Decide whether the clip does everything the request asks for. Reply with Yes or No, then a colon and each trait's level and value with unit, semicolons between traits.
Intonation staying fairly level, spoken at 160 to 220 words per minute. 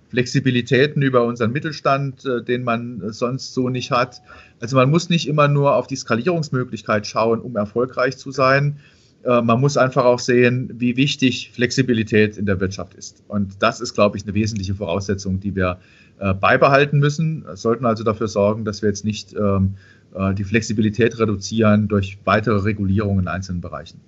No: average, 3.8 semitones; average, 165 wpm